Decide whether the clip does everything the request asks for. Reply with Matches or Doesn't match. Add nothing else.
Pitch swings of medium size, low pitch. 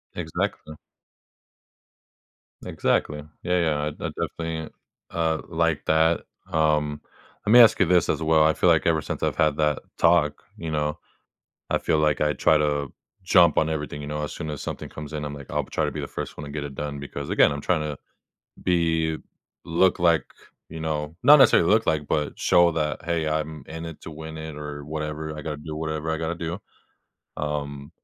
Doesn't match